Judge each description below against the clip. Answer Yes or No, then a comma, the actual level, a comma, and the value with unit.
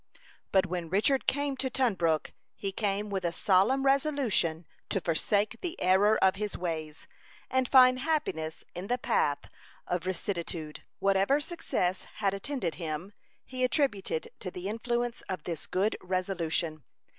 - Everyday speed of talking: Yes, average, 145 wpm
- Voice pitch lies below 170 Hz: No, high, 195 Hz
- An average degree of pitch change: No, wide, 6.3 semitones